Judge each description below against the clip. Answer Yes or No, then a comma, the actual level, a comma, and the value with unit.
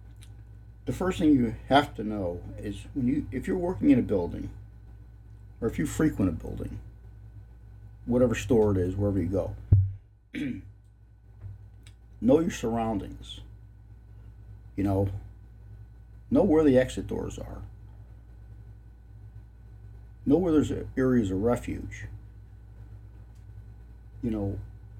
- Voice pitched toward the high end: No, low, 105 Hz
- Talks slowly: Yes, slow, 115 wpm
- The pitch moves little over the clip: Yes, narrow, 0.8 semitones